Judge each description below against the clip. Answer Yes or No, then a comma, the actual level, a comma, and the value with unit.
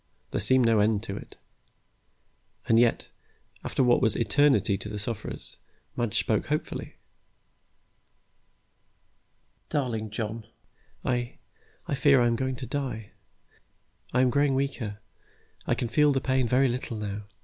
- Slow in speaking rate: No, average, 150 wpm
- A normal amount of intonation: Yes, average, 3.2 semitones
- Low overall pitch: Yes, low, 120 Hz